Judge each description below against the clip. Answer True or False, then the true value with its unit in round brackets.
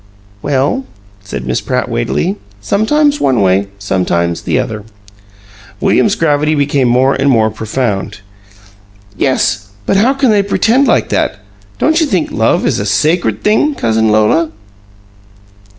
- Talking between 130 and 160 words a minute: True (135 wpm)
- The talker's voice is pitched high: False (130 Hz)